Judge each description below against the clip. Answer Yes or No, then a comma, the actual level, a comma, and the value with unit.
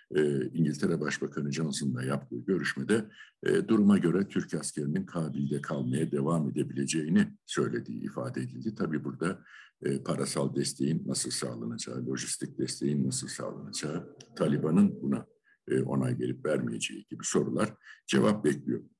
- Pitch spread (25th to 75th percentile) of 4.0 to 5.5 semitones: No, average, 3.6 semitones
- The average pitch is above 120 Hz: No, very low, 70 Hz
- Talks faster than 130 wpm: No, average, 125 wpm